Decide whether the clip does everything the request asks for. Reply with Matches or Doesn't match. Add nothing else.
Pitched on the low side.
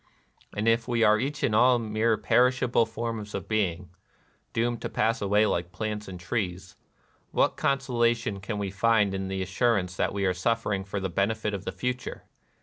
Matches